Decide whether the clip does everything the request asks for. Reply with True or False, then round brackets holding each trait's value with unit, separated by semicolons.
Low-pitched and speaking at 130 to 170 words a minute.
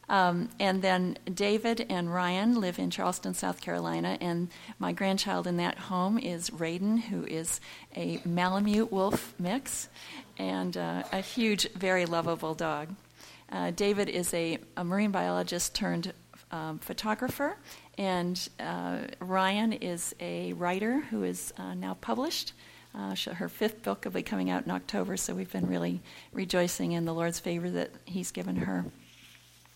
False (180 Hz; 155 wpm)